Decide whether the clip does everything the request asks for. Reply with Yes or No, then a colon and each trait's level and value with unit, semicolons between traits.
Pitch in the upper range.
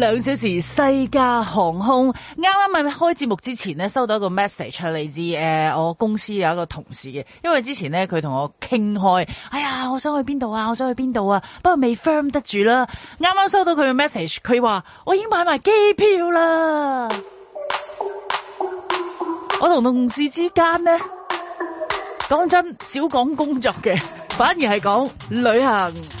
Yes: very high, 260 Hz